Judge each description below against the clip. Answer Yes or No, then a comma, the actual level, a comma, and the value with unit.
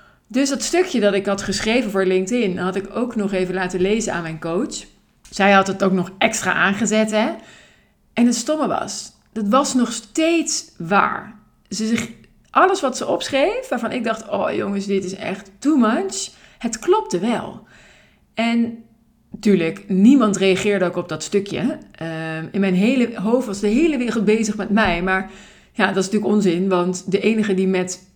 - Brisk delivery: No, average, 185 wpm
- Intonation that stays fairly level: No, average, 3.6 semitones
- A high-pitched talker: Yes, high, 210 Hz